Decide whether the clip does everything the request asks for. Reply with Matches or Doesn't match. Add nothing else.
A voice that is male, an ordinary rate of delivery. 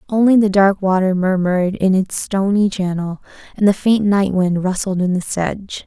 Doesn't match